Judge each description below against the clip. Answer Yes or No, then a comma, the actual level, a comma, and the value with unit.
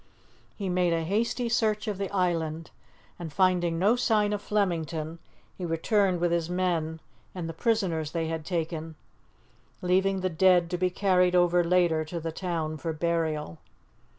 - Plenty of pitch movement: No, narrow, 2.6 semitones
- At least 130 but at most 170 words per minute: Yes, average, 160 wpm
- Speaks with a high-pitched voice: No, medium, 175 Hz